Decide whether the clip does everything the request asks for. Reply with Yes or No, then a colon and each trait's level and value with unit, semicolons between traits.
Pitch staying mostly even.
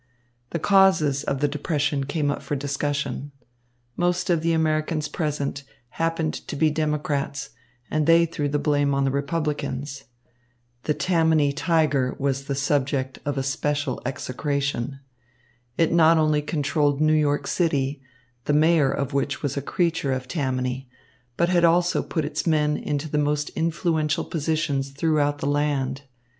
Yes: narrow, 2.2 semitones